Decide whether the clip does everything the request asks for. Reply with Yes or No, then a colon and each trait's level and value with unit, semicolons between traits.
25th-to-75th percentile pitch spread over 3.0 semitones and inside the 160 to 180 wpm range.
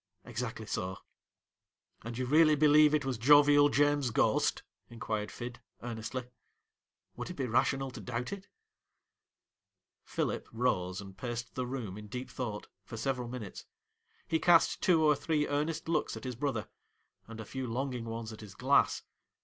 Yes: average, 4.3 semitones; average, 170 wpm